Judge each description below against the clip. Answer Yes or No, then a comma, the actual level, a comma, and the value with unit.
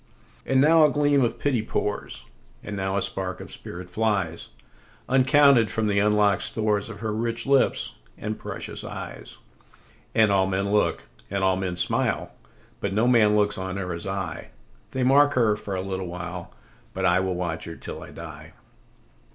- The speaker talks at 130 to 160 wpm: Yes, average, 155 wpm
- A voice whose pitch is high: No, low, 105 Hz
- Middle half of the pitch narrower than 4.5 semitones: Yes, average, 3.6 semitones